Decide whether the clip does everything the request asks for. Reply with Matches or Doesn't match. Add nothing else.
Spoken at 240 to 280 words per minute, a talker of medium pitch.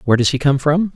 Doesn't match